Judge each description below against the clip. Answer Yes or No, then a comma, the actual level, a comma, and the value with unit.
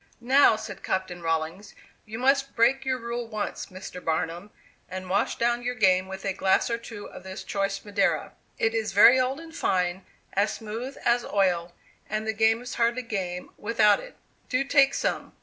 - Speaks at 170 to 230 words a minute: Yes, average, 185 wpm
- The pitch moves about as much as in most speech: Yes, average, 4.3 semitones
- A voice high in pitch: Yes, high, 215 Hz